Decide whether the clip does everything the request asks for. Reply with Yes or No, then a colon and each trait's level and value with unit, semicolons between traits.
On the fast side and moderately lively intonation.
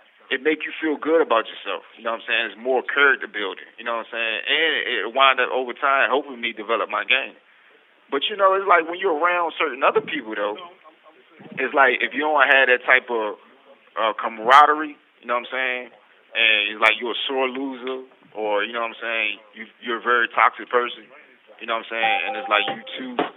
No: fast, 230 wpm; wide, 6.4 semitones